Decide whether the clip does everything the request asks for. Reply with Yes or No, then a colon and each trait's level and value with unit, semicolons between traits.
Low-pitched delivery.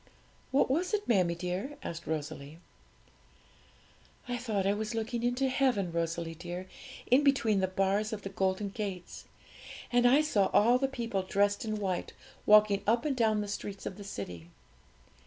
No: high, 205 Hz